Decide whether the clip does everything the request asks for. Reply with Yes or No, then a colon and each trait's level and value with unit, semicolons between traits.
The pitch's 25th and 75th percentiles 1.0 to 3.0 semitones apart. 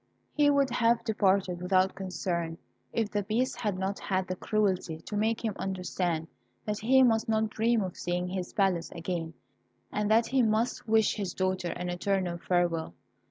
No: average, 3.6 semitones